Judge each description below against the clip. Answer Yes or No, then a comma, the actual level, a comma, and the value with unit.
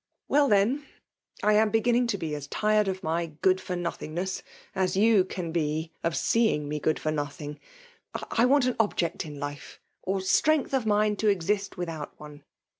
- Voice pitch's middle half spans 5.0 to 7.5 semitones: Yes, average, 5.3 semitones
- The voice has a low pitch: No, high, 190 Hz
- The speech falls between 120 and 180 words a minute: No, average, 190 wpm